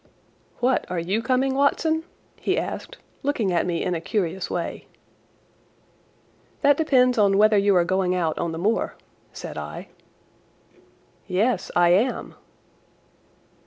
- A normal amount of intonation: No, wide, 6.1 semitones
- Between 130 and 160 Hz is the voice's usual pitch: No, high, 200 Hz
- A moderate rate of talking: No, slow, 125 wpm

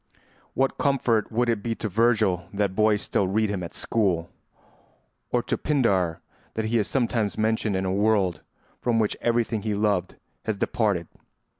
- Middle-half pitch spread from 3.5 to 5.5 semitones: No, average, 2.9 semitones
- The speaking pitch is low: Yes, low, 110 Hz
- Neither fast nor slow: Yes, average, 165 wpm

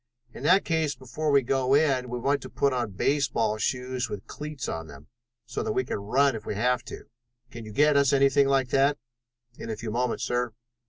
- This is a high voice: No, low, 130 Hz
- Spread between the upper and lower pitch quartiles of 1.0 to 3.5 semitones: Yes, average, 3.1 semitones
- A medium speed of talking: No, fast, 215 wpm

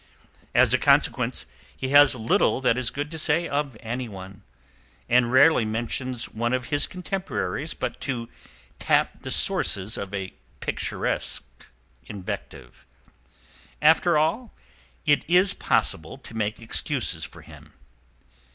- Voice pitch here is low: Yes, low, 130 Hz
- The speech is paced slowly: Yes, slow, 125 wpm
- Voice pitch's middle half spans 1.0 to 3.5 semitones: No, average, 5.1 semitones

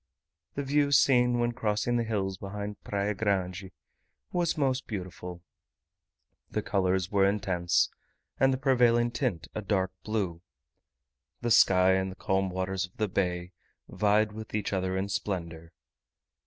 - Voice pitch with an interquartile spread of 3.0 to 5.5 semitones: Yes, average, 3.9 semitones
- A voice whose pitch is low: Yes, low, 100 Hz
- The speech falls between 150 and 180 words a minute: No, average, 140 wpm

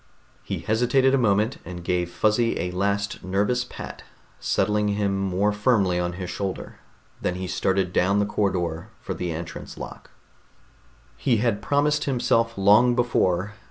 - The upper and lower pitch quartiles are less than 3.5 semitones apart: No, average, 4.0 semitones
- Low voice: Yes, low, 100 Hz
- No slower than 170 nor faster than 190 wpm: No, average, 150 wpm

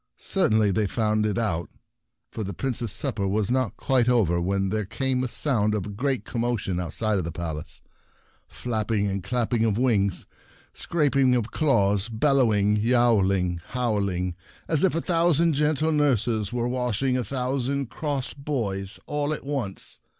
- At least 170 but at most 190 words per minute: No, average, 160 wpm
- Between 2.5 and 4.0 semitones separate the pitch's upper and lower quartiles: No, average, 4.8 semitones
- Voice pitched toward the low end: Yes, low, 115 Hz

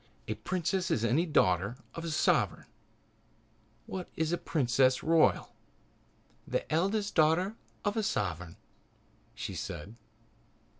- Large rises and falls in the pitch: Yes, wide, 7.3 semitones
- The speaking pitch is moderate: Yes, medium, 160 Hz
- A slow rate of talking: Yes, slow, 115 wpm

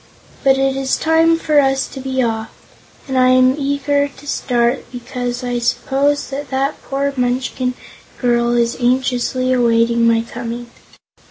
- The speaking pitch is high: Yes, very high, 255 Hz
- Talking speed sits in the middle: Yes, average, 150 wpm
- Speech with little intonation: Yes, narrow, 2.1 semitones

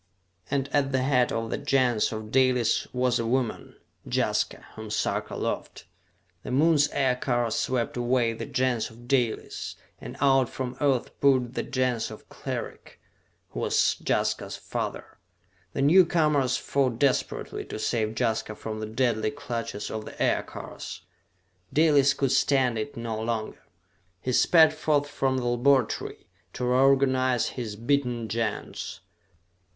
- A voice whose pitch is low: Yes, low, 125 Hz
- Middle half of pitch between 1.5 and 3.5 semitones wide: Yes, average, 3.0 semitones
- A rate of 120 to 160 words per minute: Yes, average, 140 wpm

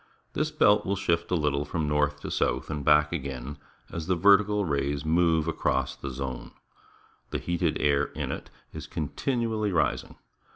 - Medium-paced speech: Yes, average, 170 wpm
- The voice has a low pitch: Yes, very low, 80 Hz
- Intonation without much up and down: No, average, 4.0 semitones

